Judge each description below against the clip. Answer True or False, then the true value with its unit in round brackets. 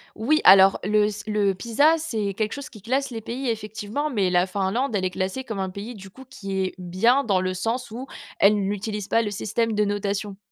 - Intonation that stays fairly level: False (3.2 semitones)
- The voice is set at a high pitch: True (210 Hz)